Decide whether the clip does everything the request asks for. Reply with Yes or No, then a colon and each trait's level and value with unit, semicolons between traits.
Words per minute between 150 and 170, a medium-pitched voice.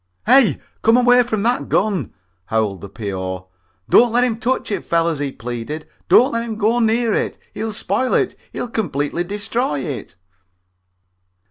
No: average, 160 wpm; high, 210 Hz